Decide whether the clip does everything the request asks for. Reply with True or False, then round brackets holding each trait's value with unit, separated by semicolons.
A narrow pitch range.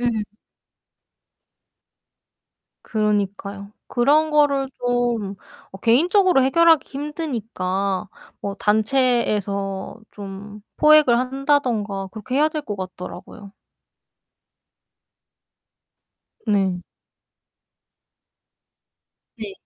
False (5.4 semitones)